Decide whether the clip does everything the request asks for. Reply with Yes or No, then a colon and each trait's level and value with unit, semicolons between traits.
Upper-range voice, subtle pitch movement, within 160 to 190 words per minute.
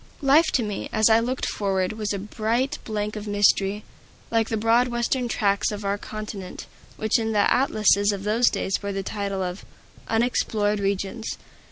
Yes: high, 210 Hz; narrow, 2.1 semitones; average, 175 wpm